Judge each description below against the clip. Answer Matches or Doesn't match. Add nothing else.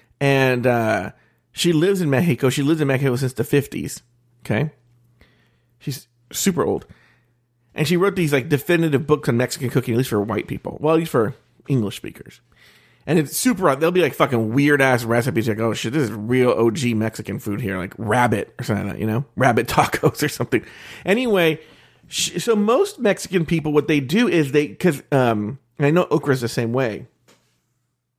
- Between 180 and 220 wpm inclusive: Matches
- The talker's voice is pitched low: Matches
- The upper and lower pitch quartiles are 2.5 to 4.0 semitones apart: Doesn't match